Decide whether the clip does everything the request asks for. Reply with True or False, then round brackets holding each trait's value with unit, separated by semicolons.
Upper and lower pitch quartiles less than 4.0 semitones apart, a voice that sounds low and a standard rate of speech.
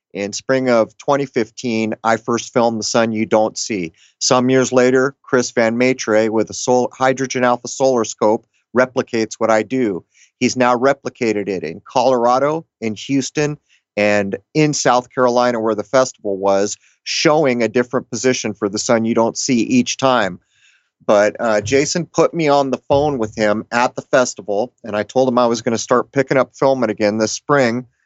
True (2.9 semitones; 125 Hz; 180 wpm)